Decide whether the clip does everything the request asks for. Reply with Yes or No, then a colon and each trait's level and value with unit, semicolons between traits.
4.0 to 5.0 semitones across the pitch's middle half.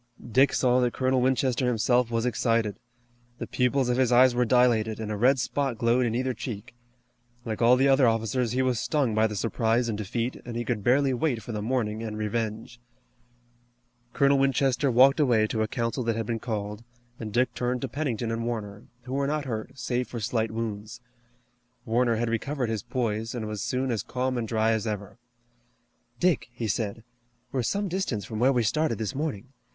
No: narrow, 2.6 semitones